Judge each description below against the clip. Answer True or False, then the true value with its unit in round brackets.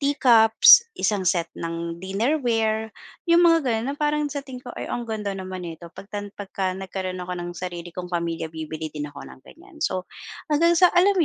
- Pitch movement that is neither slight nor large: False (7.2 semitones)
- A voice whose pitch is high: True (200 Hz)